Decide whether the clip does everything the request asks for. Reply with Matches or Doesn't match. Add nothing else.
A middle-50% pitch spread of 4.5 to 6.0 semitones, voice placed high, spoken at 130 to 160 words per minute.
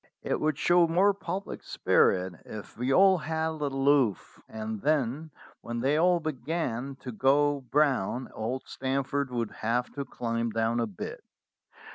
Doesn't match